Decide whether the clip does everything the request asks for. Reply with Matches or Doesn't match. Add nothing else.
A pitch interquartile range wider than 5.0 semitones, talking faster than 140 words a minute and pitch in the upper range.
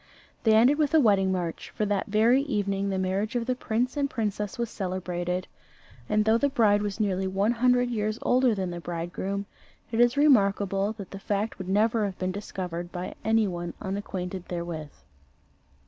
Doesn't match